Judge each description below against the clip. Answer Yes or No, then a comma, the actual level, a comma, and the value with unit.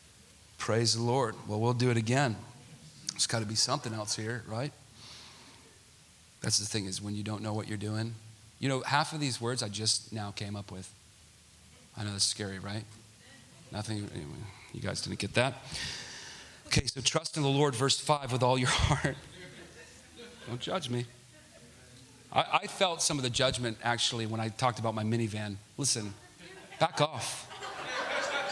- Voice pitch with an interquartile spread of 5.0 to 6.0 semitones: No, average, 3.5 semitones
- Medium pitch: No, low, 115 Hz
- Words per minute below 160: No, average, 175 wpm